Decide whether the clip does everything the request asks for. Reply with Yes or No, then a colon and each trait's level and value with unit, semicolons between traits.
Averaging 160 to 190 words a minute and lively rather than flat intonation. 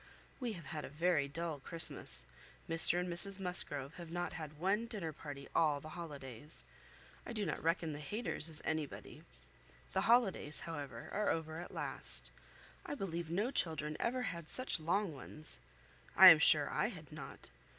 No: average, 170 wpm; average, 3.7 semitones